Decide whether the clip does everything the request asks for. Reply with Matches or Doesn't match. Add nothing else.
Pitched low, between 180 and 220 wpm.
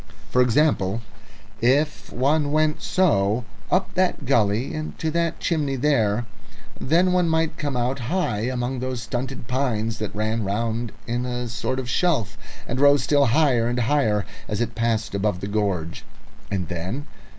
Doesn't match